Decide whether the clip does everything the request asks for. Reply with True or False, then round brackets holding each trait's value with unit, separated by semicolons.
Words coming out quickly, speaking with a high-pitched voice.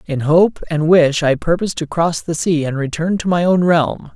False (230 wpm; 165 Hz)